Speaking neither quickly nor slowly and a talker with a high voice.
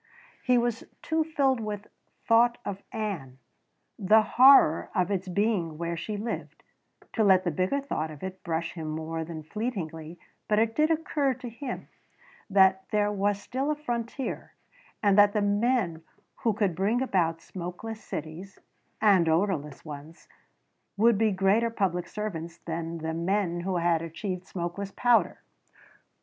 Yes: average, 150 wpm; high, 195 Hz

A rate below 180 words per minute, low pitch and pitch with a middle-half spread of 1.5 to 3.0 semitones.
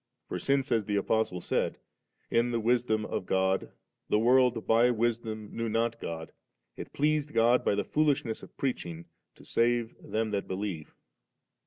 Yes: average, 165 wpm; low, 115 Hz; average, 2.7 semitones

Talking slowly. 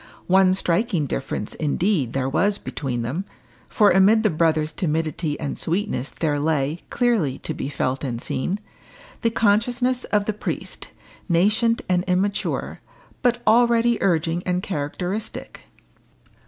Yes: slow, 130 wpm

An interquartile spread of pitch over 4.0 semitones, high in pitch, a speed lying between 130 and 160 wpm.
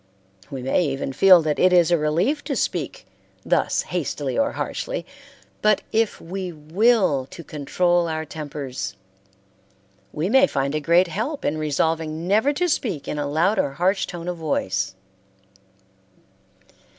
No: average, 4.6 semitones; medium, 165 Hz; average, 150 wpm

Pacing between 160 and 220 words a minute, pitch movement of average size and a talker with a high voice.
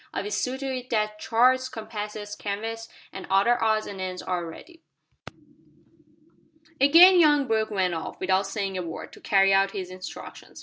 Yes: average, 165 wpm; average, 4.1 semitones; high, 210 Hz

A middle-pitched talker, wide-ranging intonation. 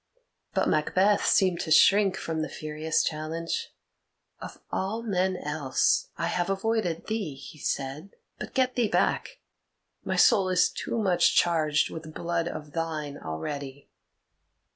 No: medium, 165 Hz; average, 4.1 semitones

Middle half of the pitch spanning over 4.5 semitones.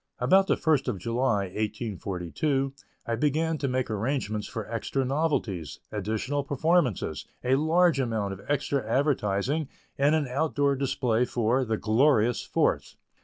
Yes: average, 4.9 semitones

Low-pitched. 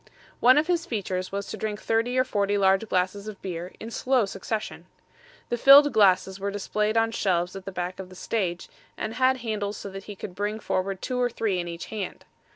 No: high, 205 Hz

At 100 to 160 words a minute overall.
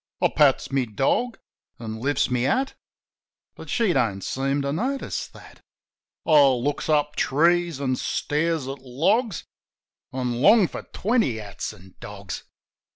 Yes: average, 140 wpm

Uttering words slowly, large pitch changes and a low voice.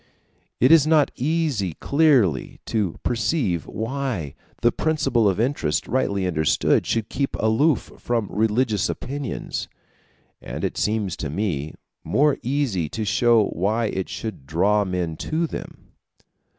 Yes: slow, 130 wpm; wide, 6.4 semitones; low, 110 Hz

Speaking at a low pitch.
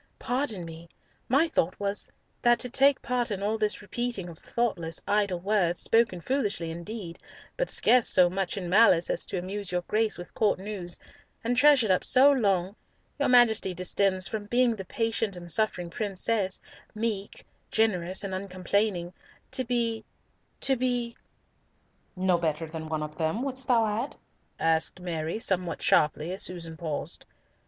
No: high, 200 Hz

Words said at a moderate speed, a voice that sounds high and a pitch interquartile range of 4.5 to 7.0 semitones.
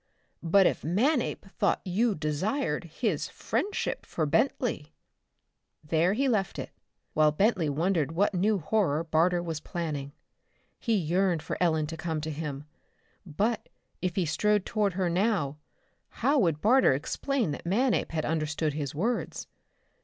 No: average, 145 wpm; medium, 175 Hz; average, 5.2 semitones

